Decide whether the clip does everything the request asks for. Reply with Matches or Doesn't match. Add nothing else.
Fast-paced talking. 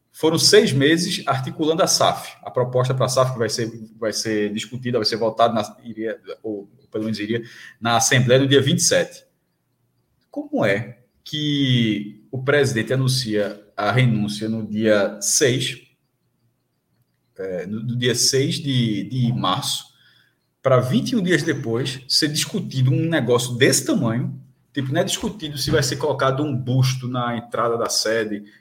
Doesn't match